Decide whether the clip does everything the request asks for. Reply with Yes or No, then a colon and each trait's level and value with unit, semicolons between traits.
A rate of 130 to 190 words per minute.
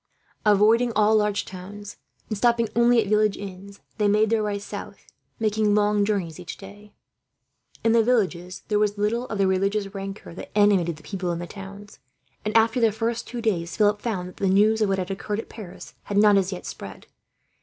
No: average, 200 wpm